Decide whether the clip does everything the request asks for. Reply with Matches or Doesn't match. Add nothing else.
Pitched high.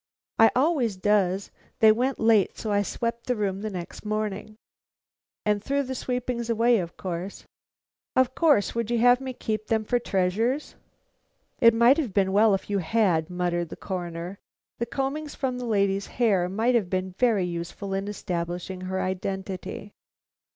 Matches